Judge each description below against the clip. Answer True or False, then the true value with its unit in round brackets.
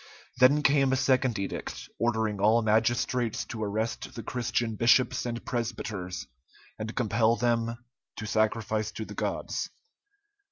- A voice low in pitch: True (115 Hz)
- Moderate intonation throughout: False (1.9 semitones)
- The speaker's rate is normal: False (130 wpm)